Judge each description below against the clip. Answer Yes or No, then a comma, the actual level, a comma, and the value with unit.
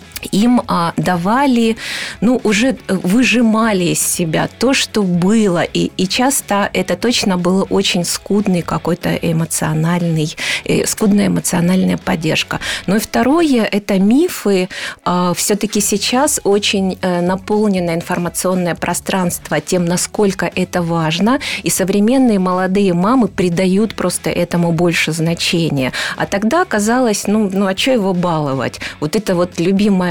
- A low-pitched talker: No, high, 190 Hz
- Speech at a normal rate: Yes, average, 125 wpm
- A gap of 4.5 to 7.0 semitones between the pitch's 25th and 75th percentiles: No, average, 3.7 semitones